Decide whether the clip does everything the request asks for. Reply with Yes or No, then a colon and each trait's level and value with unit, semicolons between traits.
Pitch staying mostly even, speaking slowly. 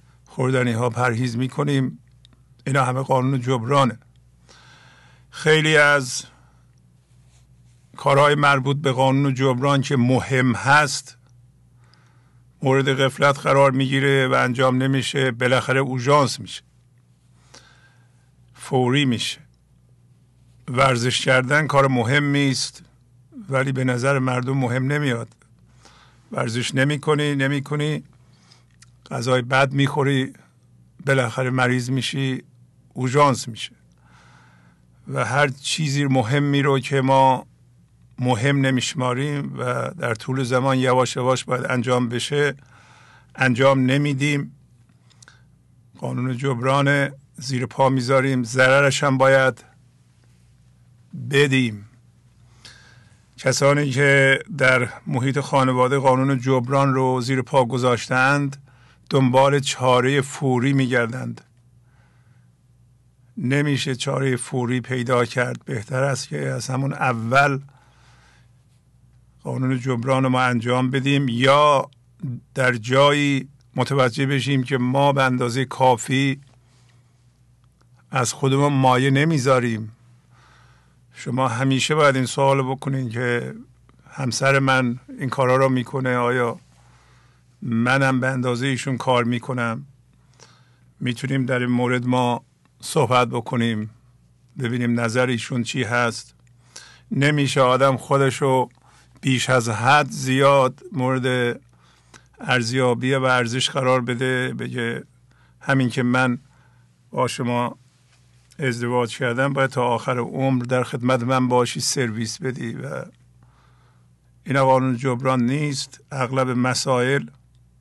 Yes: narrow, 1.7 semitones; slow, 100 wpm